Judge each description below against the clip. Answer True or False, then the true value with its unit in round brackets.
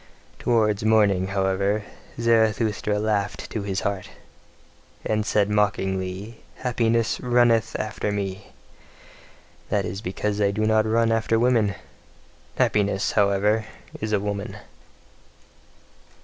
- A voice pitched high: False (105 Hz)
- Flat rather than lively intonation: True (1.9 semitones)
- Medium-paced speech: False (105 wpm)